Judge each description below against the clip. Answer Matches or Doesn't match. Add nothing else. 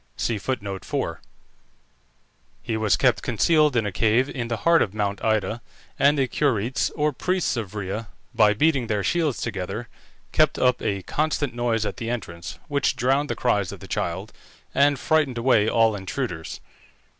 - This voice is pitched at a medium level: Doesn't match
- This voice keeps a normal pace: Matches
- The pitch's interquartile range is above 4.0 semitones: Matches